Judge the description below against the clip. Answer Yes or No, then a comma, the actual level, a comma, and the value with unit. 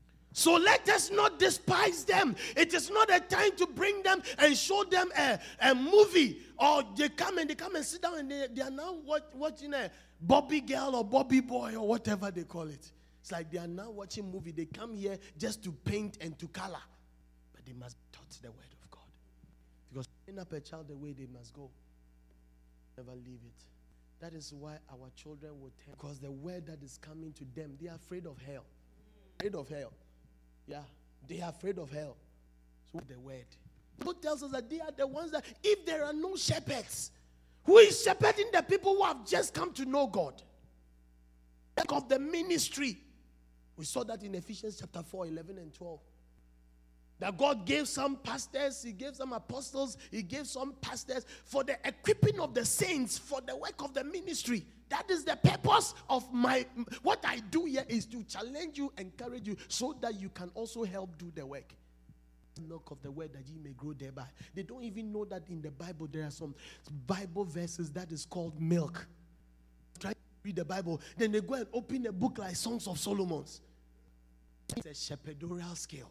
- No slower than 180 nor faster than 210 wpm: Yes, average, 200 wpm